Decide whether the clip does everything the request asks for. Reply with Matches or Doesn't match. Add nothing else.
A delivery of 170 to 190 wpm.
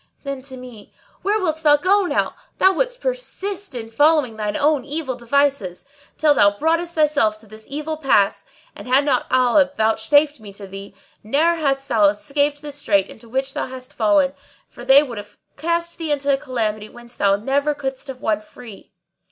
Matches